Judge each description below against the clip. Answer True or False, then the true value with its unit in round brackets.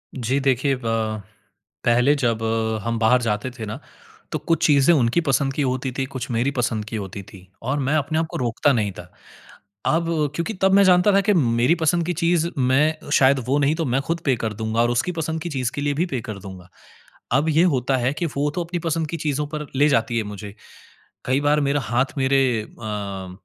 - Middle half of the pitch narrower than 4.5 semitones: False (4.9 semitones)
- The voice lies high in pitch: False (135 Hz)